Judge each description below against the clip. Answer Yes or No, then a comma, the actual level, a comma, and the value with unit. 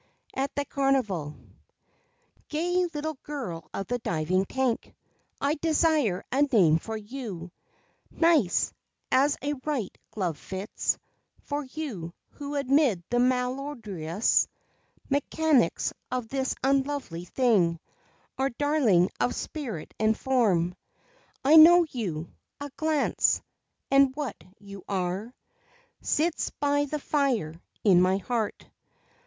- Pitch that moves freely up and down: Yes, wide, 7.0 semitones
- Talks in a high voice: Yes, very high, 255 Hz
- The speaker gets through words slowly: Yes, slow, 115 wpm